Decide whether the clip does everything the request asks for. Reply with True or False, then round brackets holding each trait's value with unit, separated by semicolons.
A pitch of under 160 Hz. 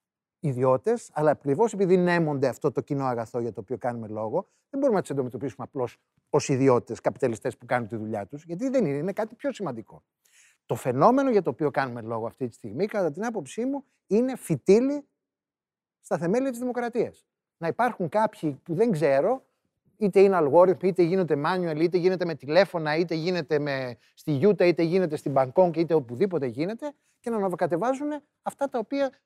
False (175 Hz)